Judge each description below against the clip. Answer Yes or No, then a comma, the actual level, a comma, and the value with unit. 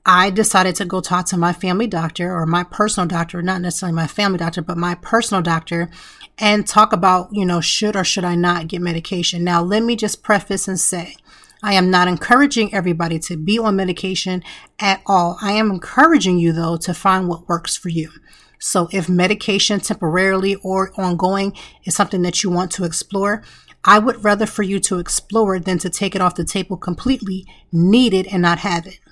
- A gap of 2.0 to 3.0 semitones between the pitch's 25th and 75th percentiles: Yes, narrow, 2.4 semitones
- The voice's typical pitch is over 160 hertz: Yes, medium, 185 Hz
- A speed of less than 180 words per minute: No, average, 200 wpm